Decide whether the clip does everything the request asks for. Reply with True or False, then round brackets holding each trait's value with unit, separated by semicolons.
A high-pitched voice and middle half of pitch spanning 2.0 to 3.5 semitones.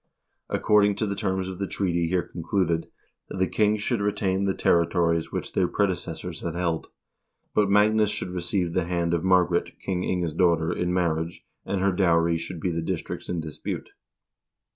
False (90 Hz; 2.6 semitones)